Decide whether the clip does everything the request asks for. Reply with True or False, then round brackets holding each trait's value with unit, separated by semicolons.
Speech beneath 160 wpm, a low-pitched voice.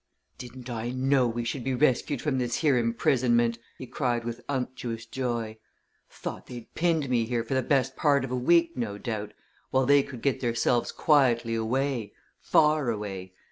False (170 wpm; 125 Hz)